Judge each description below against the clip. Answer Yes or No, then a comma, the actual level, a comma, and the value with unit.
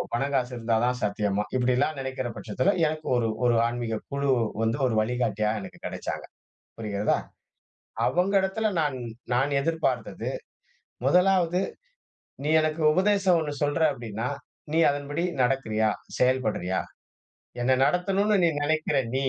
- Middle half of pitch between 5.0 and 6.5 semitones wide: Yes, wide, 5.4 semitones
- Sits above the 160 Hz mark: No, low, 135 Hz